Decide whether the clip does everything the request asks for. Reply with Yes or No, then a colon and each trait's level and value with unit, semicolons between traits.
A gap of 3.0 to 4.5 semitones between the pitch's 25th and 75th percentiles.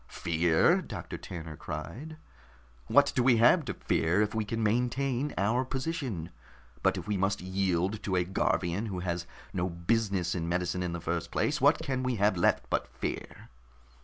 No: wide, 5.6 semitones